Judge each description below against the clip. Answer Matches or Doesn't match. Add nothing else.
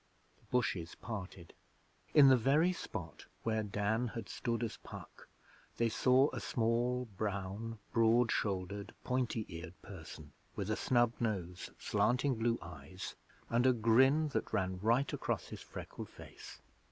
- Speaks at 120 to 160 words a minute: Matches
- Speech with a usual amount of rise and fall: Matches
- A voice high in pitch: Doesn't match